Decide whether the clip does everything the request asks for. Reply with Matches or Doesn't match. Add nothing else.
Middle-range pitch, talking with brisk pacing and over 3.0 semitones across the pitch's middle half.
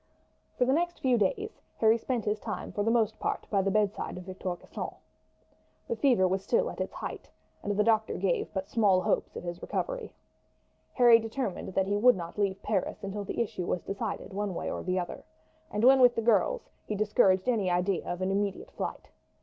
Doesn't match